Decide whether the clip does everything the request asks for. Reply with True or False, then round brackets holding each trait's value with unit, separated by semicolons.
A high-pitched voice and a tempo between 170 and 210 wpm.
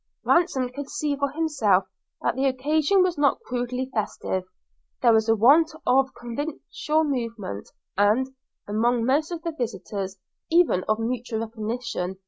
False (250 Hz; 140 wpm)